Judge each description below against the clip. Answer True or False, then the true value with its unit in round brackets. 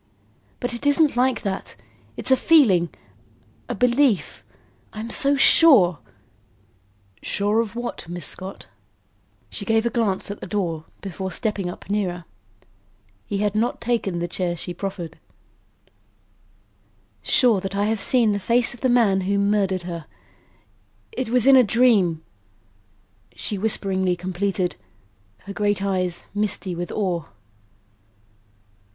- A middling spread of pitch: True (4.4 semitones)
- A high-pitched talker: True (200 Hz)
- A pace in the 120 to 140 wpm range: True (135 wpm)